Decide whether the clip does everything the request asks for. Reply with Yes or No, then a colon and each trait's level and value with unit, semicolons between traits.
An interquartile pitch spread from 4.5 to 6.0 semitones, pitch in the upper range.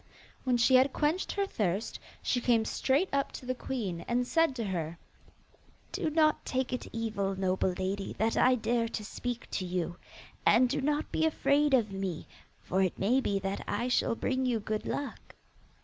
Yes: average, 5.2 semitones; high, 235 Hz